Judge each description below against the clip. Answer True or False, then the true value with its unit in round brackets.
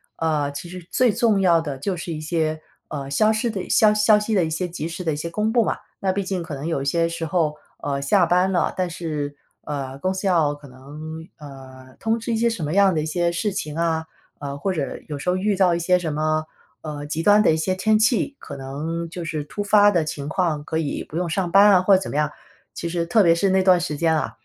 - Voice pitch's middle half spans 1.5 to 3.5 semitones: False (4.0 semitones)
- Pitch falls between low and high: True (170 Hz)